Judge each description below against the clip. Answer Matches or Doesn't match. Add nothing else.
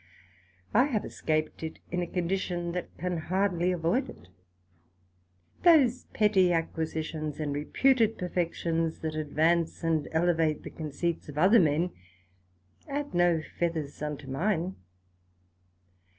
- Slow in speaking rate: Matches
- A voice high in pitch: Doesn't match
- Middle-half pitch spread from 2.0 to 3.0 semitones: Matches